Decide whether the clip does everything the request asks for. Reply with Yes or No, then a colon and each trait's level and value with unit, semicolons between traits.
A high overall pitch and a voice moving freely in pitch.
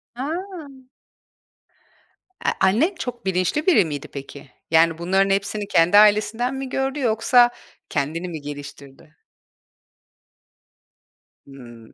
Yes: high, 195 Hz; wide, 8.4 semitones